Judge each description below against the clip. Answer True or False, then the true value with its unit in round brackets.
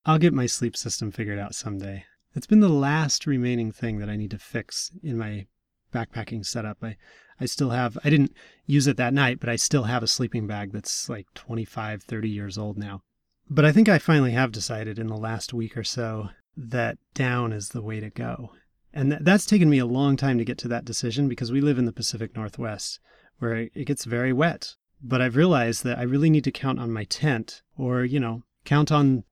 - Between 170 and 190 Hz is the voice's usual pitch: False (120 Hz)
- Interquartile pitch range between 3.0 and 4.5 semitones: True (4.1 semitones)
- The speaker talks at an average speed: False (225 wpm)